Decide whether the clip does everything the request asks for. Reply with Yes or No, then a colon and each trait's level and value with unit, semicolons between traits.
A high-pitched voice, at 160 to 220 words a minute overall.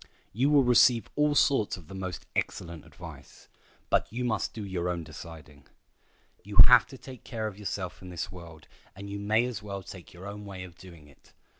No: low, 100 Hz; average, 200 wpm